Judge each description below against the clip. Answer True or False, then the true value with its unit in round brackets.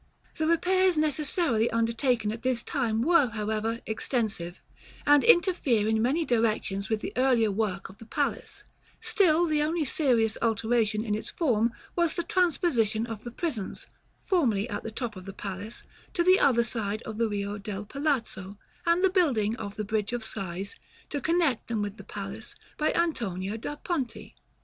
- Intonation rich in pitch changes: True (6.1 semitones)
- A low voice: False (230 Hz)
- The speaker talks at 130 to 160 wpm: False (175 wpm)